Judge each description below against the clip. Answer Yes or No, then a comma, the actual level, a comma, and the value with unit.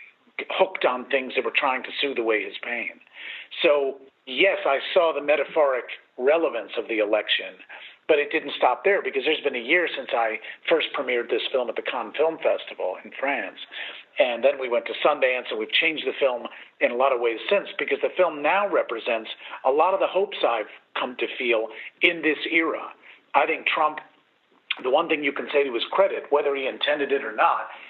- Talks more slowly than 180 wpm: No, fast, 205 wpm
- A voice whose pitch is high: Yes, high, 200 Hz